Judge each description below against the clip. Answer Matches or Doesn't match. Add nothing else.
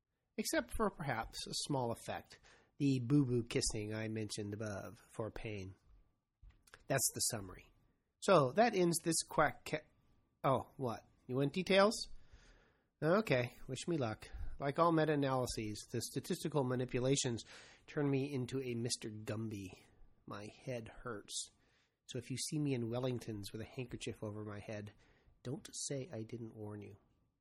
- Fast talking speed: Doesn't match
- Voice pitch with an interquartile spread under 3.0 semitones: Doesn't match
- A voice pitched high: Doesn't match